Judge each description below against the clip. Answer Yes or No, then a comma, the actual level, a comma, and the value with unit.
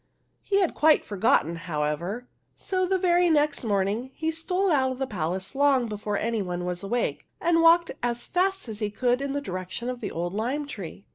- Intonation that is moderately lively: No, wide, 8.3 semitones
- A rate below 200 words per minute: No, fast, 205 wpm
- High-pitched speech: Yes, high, 245 Hz